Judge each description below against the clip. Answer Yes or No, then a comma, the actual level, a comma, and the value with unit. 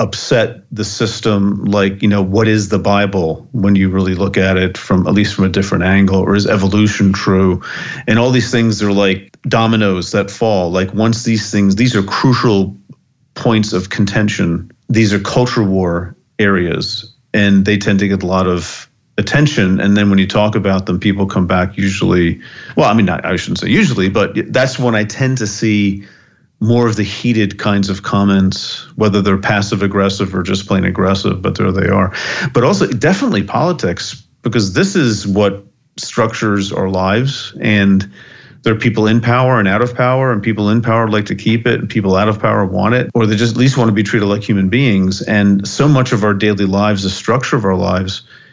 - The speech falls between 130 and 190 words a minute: No, fast, 205 wpm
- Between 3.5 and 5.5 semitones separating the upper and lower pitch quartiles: No, average, 2.7 semitones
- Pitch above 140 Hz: No, low, 105 Hz